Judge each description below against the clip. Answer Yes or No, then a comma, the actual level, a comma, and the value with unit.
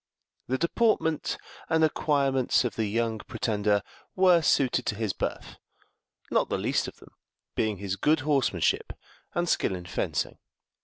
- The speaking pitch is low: Yes, low, 130 Hz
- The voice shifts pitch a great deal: Yes, wide, 7.0 semitones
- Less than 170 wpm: Yes, average, 145 wpm